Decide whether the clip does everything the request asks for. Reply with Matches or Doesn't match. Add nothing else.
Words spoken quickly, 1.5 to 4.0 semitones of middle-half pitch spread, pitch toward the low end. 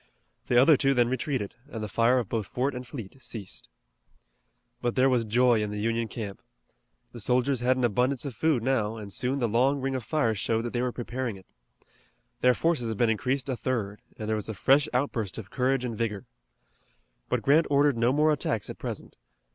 Matches